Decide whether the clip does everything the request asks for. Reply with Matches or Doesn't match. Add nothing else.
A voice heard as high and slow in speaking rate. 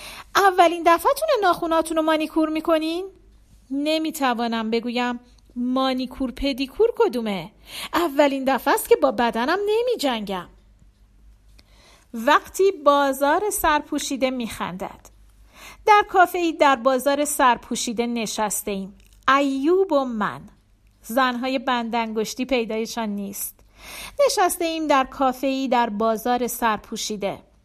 Matches